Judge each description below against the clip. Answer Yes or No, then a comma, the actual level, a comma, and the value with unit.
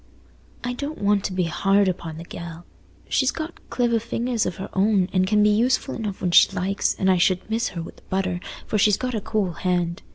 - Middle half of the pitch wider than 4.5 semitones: No, average, 3.7 semitones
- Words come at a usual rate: No, fast, 225 wpm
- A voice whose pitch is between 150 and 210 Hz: Yes, high, 195 Hz